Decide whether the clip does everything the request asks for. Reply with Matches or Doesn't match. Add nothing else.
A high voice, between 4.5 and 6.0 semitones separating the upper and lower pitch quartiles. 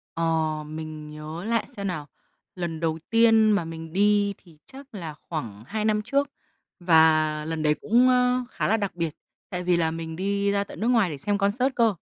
Doesn't match